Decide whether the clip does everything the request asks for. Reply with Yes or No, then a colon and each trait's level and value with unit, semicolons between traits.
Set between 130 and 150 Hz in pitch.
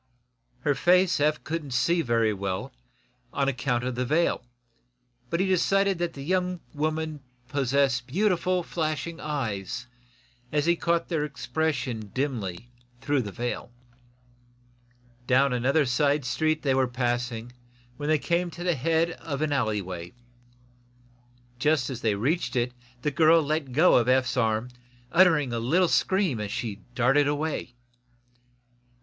Yes: medium, 140 Hz